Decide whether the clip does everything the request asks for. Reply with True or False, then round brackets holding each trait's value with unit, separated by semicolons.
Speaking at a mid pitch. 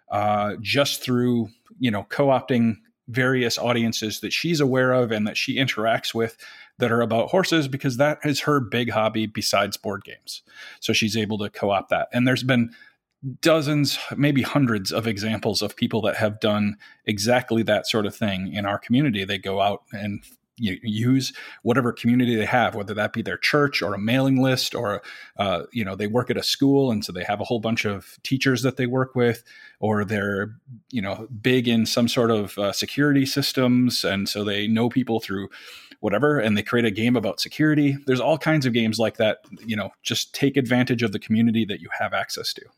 False (115 Hz)